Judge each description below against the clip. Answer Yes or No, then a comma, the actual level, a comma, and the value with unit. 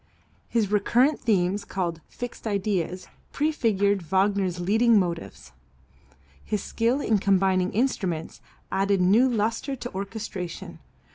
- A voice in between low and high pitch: No, high, 200 Hz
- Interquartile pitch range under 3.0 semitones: No, average, 3.7 semitones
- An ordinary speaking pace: No, slow, 110 wpm